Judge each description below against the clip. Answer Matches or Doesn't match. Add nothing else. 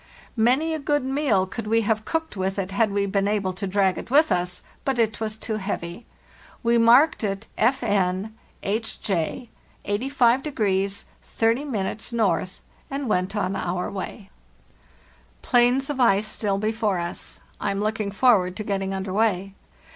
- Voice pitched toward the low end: Doesn't match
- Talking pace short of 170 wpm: Matches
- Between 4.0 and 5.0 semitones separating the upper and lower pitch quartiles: Doesn't match